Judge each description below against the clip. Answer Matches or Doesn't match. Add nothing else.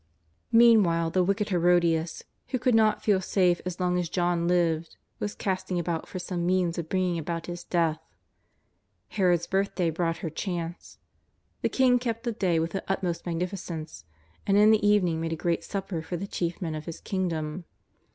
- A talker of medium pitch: Matches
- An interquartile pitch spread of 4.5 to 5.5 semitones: Doesn't match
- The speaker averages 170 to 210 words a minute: Matches